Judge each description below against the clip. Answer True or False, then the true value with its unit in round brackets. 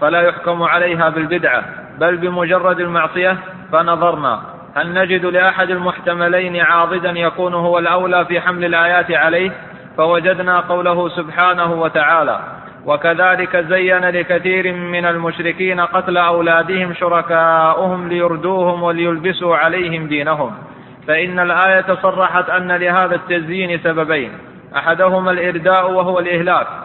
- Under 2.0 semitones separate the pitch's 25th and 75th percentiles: True (1.4 semitones)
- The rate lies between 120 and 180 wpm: False (105 wpm)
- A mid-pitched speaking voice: True (175 Hz)